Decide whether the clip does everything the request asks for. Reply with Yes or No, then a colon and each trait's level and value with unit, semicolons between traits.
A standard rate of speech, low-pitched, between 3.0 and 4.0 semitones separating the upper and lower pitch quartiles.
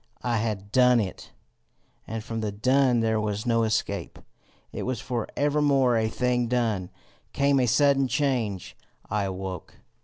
Yes: average, 150 wpm; low, 115 Hz; average, 3.3 semitones